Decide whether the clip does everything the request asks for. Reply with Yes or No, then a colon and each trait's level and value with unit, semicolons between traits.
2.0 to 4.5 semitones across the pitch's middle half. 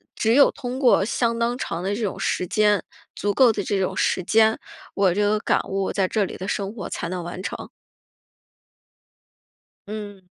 Yes: average, 2.7 semitones